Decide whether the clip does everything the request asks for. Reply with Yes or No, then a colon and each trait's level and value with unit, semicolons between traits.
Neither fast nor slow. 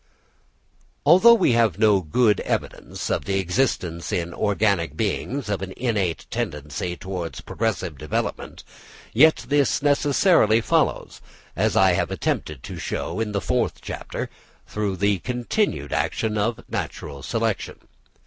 No: slow, 130 wpm